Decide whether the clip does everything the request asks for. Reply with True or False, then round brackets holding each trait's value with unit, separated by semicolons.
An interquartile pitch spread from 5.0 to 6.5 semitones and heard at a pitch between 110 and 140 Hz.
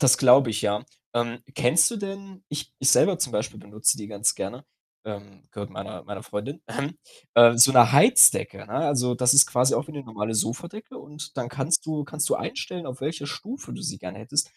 True (5.4 semitones; 135 Hz)